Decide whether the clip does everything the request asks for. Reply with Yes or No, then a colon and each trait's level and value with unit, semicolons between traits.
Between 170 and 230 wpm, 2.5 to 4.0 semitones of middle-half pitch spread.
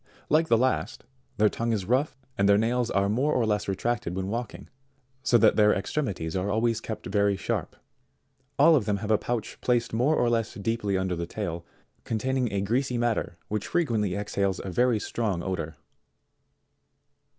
Yes: average, 180 wpm; average, 3.5 semitones